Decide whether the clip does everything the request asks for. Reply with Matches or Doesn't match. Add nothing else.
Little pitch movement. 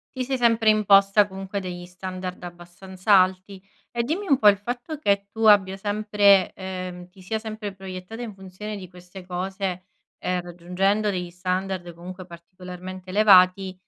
Matches